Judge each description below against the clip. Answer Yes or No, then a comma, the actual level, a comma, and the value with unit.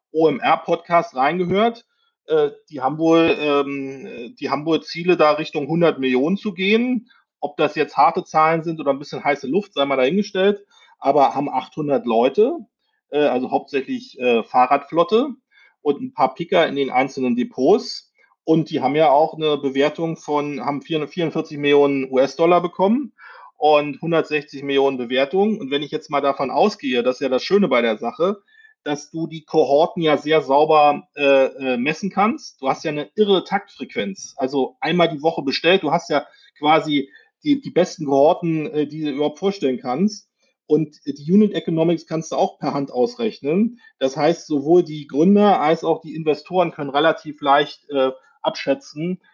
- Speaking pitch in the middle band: Yes, medium, 155 Hz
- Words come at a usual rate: Yes, average, 165 wpm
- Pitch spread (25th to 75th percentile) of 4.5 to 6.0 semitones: Yes, average, 4.9 semitones